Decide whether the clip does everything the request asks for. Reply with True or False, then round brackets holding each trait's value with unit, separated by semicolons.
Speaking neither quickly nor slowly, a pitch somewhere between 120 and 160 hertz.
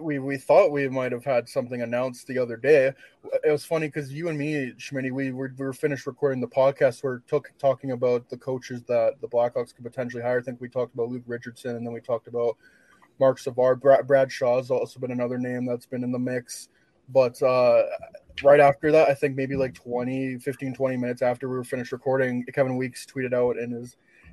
False (220 wpm; 130 Hz)